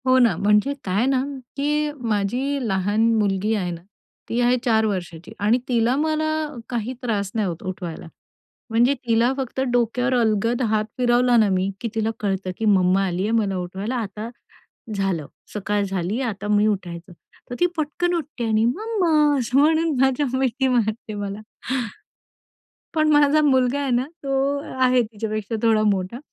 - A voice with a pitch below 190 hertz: No, high, 225 Hz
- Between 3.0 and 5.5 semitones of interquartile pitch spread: Yes, average, 4.4 semitones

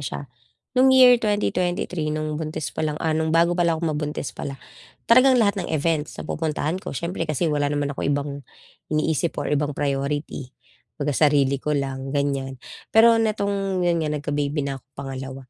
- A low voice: No, medium, 155 Hz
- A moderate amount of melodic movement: Yes, average, 3.5 semitones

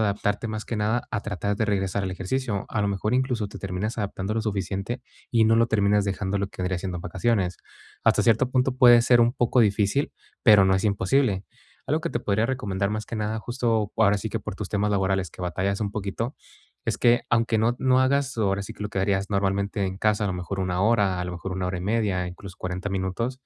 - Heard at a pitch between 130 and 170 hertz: No, low, 105 Hz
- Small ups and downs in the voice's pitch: No, average, 3.1 semitones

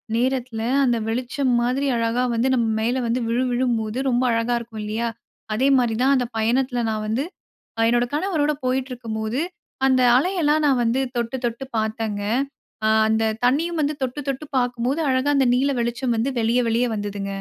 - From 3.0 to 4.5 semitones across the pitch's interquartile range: No, narrow, 2.5 semitones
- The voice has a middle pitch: No, high, 245 Hz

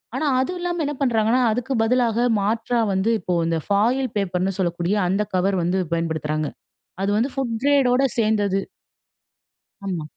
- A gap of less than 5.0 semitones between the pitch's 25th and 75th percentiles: No, average, 5.3 semitones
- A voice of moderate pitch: No, high, 215 Hz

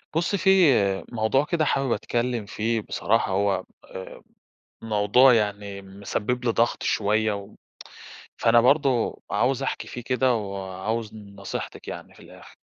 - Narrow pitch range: No, average, 3.5 semitones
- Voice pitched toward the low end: Yes, low, 110 Hz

